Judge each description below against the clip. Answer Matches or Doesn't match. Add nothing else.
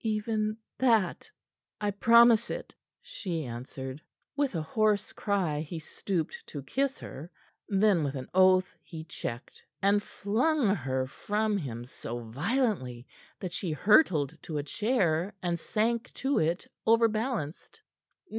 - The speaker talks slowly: Matches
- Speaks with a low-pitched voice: Doesn't match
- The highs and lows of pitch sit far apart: Matches